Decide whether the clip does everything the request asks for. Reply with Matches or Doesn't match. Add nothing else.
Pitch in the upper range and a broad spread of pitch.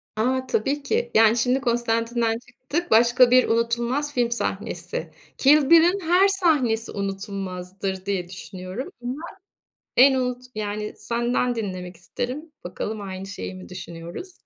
Doesn't match